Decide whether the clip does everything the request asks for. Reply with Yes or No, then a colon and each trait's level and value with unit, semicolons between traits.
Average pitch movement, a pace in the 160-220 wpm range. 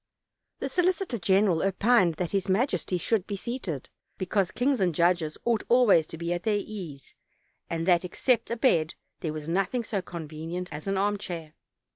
Yes: average, 4.7 semitones; average, 170 wpm